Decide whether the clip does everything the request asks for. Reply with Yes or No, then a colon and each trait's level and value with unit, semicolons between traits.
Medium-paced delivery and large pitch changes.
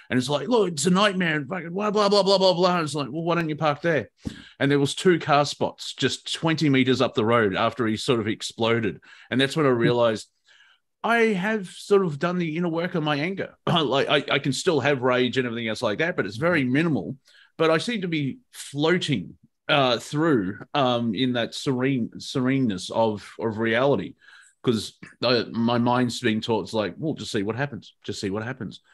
No: fast, 220 wpm; wide, 6.0 semitones